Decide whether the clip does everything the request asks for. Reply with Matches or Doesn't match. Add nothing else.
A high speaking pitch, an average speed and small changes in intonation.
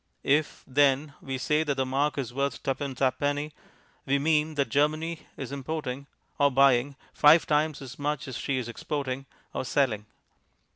Doesn't match